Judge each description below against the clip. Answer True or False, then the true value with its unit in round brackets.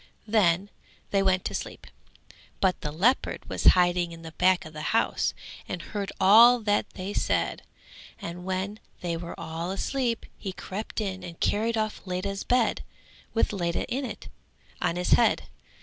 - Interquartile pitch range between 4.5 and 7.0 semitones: False (3.5 semitones)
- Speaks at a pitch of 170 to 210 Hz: True (190 Hz)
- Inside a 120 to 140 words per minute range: False (165 wpm)